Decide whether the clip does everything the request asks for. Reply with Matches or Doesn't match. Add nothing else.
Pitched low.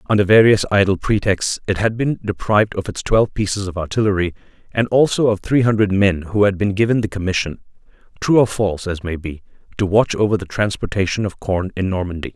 Matches